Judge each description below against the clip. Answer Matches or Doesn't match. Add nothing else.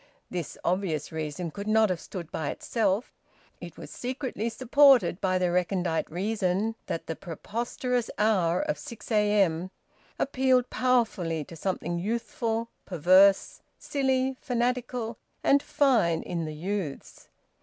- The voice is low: Doesn't match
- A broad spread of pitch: Matches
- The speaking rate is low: Matches